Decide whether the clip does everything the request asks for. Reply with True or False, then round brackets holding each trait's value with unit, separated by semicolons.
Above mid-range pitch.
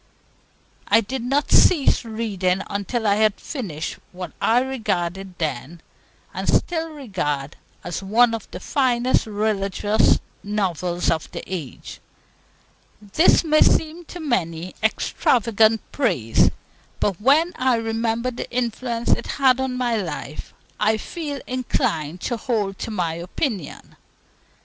True (220 Hz)